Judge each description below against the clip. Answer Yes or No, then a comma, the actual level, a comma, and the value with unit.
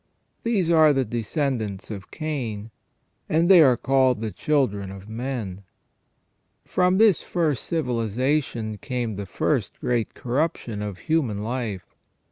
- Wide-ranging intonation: Yes, wide, 6.1 semitones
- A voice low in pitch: Yes, low, 125 Hz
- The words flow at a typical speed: No, slow, 125 wpm